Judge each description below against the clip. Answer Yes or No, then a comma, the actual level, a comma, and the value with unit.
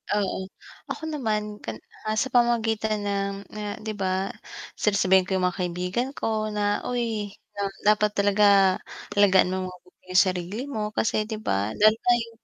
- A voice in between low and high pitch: No, high, 210 Hz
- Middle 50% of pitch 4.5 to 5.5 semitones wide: No, narrow, 2.4 semitones